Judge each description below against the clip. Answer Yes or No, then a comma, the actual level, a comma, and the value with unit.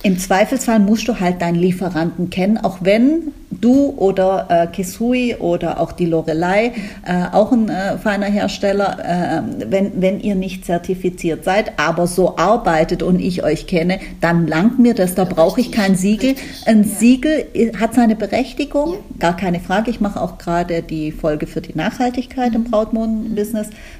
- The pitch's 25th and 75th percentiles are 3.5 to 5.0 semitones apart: Yes, average, 4.5 semitones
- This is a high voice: Yes, high, 195 Hz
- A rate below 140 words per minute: No, average, 165 wpm